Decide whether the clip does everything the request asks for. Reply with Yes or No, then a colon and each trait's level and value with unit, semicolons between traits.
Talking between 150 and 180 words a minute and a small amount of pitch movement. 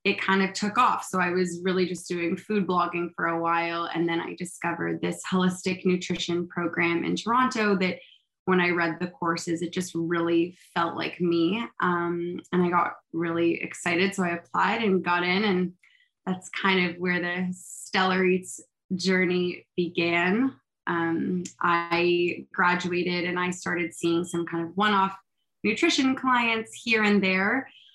Yes: average, 165 wpm; narrow, 1.8 semitones